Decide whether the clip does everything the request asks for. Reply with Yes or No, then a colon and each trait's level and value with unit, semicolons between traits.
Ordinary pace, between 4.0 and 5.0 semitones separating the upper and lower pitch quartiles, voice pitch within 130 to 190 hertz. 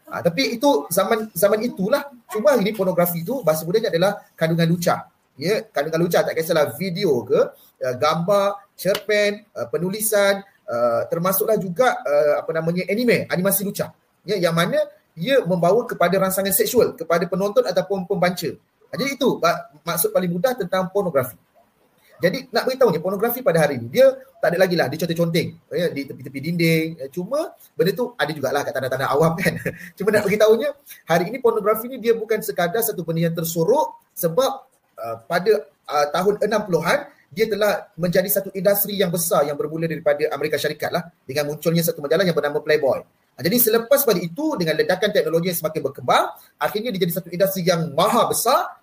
No: fast, 170 wpm; average, 4.6 semitones; medium, 185 Hz